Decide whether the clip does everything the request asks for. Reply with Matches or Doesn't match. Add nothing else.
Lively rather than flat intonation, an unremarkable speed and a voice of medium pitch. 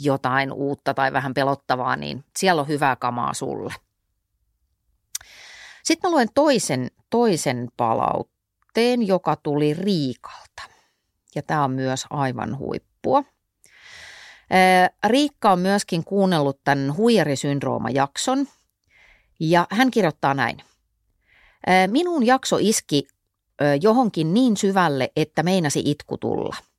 Matches